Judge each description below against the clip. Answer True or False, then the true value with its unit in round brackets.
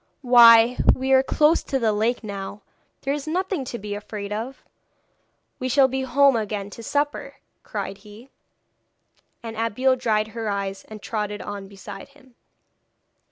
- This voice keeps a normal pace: True (155 wpm)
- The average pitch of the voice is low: False (230 Hz)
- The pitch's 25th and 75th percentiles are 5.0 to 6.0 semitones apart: False (4.2 semitones)